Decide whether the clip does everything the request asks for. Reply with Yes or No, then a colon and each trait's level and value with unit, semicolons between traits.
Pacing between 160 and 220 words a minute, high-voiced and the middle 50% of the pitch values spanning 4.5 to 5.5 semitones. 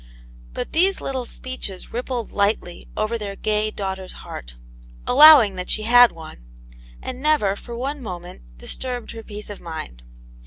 No: average, 150 wpm; high, 215 Hz; average, 4.8 semitones